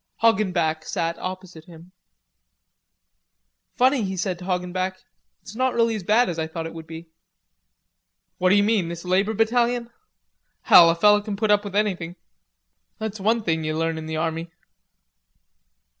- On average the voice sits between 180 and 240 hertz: Yes, medium, 185 Hz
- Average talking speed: Yes, average, 160 wpm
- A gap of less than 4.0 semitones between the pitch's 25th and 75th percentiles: No, average, 4.4 semitones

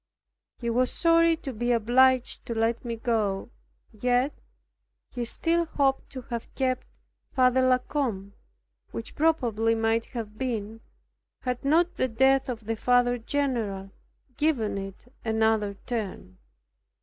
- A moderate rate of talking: No, slow, 130 wpm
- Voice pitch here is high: Yes, high, 240 Hz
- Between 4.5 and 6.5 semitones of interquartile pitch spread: No, average, 2.8 semitones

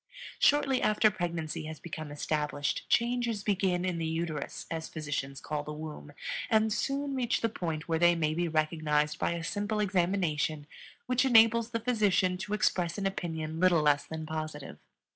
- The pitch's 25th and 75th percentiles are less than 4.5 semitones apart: No, average, 5.3 semitones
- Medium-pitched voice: Yes, medium, 170 Hz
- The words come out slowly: No, average, 165 wpm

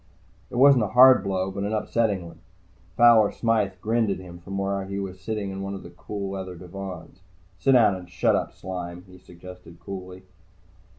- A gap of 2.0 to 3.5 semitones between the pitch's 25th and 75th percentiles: Yes, narrow, 2.5 semitones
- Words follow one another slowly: No, average, 185 wpm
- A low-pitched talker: Yes, very low, 95 Hz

